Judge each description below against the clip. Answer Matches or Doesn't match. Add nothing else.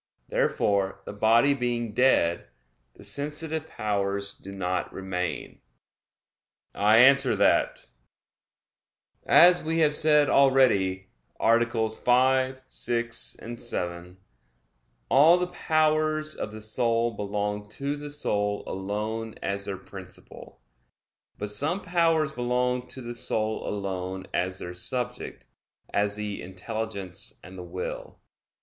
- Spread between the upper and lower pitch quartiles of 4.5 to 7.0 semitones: Matches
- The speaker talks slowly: Matches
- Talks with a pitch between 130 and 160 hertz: Doesn't match